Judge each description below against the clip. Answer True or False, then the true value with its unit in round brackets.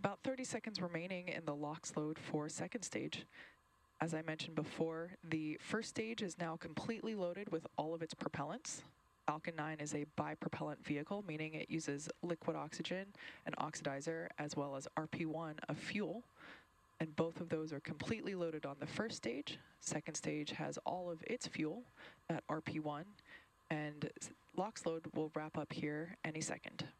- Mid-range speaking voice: True (160 Hz)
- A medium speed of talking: True (165 wpm)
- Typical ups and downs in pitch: False (2.3 semitones)